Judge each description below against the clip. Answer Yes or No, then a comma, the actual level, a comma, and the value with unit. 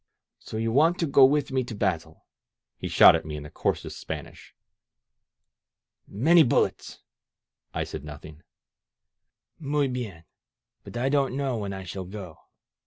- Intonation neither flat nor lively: No, wide, 7.3 semitones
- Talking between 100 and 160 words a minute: Yes, average, 150 wpm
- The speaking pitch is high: No, low, 115 Hz